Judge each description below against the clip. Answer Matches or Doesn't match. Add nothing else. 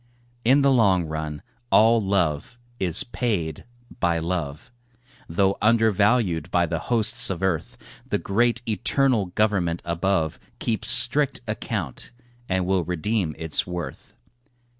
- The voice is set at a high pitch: Doesn't match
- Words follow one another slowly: Matches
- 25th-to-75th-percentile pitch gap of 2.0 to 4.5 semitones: Doesn't match